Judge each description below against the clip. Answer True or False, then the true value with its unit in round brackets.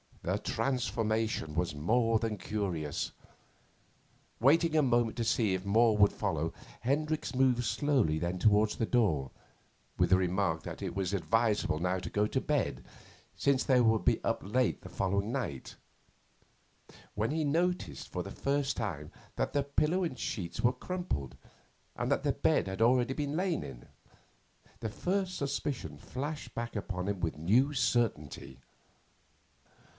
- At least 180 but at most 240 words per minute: False (150 wpm)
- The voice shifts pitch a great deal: True (6.6 semitones)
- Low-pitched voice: True (115 Hz)